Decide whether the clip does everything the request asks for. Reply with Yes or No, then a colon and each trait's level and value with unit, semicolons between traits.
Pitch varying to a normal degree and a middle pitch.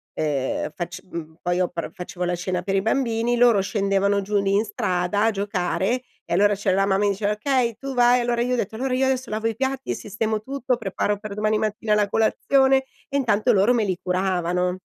No: average, 4.0 semitones; high, 210 Hz